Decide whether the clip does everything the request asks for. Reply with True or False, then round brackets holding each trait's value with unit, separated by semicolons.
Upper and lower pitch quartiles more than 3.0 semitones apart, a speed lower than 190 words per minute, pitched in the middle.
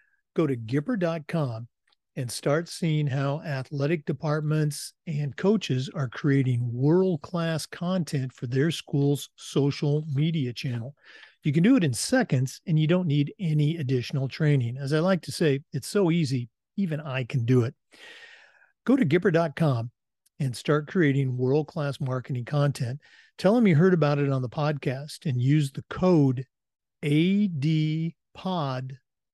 True (3.7 semitones; 145 wpm; 150 Hz)